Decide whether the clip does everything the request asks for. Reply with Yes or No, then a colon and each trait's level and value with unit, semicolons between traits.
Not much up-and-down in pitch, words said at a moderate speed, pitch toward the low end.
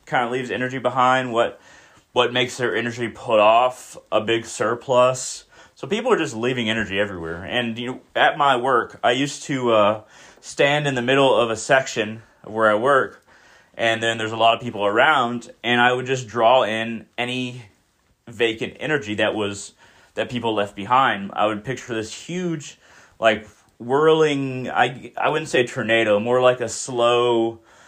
Yes: narrow, 2.3 semitones; average, 175 wpm; low, 120 Hz